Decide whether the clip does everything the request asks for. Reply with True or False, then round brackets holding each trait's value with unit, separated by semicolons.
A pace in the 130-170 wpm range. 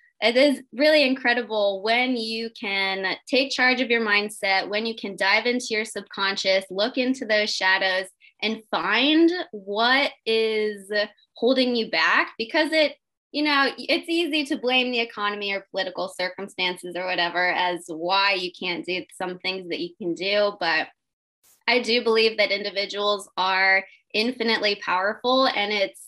True (155 wpm)